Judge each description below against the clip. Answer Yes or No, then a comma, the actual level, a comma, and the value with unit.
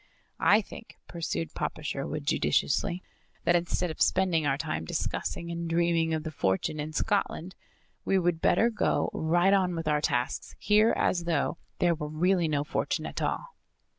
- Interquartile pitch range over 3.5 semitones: No, average, 2.8 semitones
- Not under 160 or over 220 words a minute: Yes, average, 165 wpm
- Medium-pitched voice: Yes, medium, 170 Hz